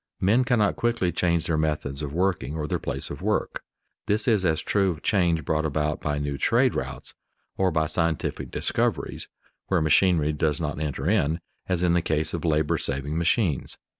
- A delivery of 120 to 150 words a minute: No, average, 185 wpm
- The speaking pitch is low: Yes, very low, 80 Hz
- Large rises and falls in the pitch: No, average, 3.3 semitones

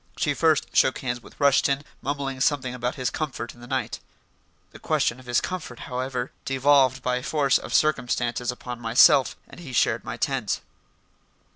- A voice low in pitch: Yes, low, 130 Hz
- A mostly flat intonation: Yes, narrow, 2.3 semitones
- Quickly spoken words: No, average, 165 wpm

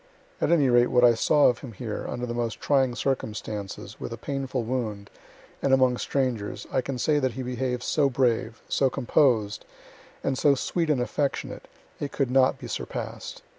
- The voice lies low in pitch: Yes, low, 125 Hz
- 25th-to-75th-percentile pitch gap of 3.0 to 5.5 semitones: No, narrow, 2.5 semitones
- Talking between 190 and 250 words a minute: No, average, 180 wpm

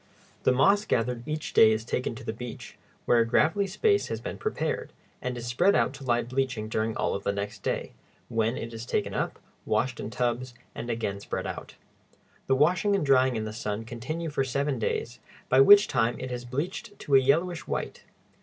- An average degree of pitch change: Yes, average, 4.2 semitones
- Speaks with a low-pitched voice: Yes, low, 125 Hz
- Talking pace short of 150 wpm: No, fast, 205 wpm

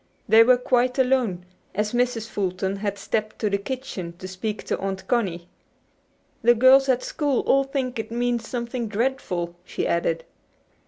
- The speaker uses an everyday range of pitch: Yes, average, 4.6 semitones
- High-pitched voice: Yes, high, 225 Hz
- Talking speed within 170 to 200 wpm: No, average, 160 wpm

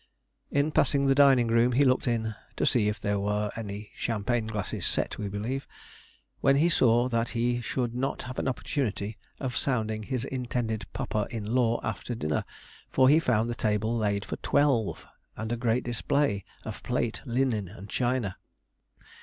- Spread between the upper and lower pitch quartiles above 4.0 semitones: No, average, 3.2 semitones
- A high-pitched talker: No, low, 115 Hz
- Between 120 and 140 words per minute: No, average, 170 wpm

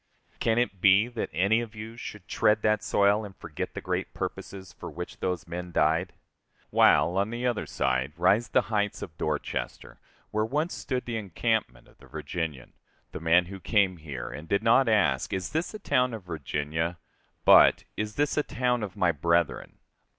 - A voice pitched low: Yes, very low, 95 Hz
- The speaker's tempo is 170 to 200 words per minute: Yes, average, 185 wpm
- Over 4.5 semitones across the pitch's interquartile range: Yes, average, 5.2 semitones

